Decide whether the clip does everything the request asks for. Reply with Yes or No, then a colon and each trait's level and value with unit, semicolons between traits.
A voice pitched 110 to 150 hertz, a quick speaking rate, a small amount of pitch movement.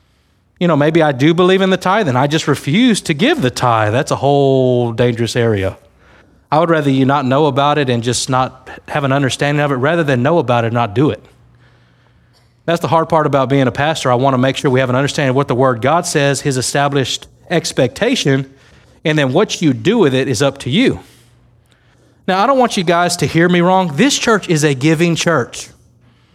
No: medium, 140 Hz; fast, 230 wpm; average, 4.6 semitones